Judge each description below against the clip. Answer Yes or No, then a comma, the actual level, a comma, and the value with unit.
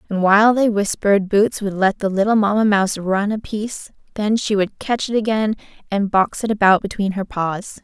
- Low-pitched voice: No, high, 205 Hz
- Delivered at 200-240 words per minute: Yes, fast, 205 wpm